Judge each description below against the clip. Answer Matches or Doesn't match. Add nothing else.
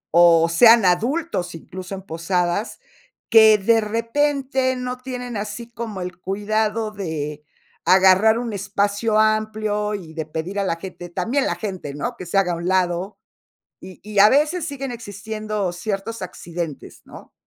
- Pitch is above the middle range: Matches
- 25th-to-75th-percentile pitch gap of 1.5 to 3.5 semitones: Doesn't match